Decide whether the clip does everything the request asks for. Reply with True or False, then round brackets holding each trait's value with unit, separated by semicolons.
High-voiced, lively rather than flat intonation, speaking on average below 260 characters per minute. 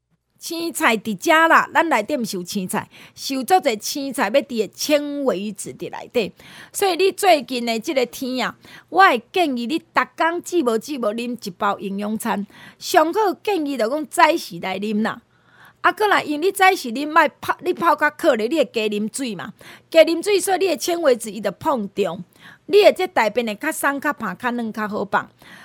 False (285 Hz; 7.2 semitones; 265 characters per minute)